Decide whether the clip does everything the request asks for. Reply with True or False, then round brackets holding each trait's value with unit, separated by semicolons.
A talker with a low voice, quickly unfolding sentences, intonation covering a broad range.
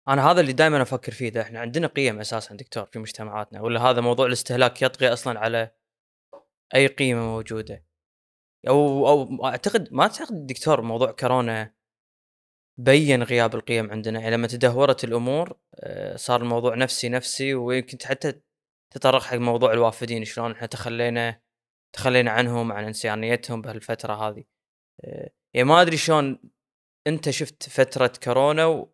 False (120 Hz; 145 wpm; 2.9 semitones)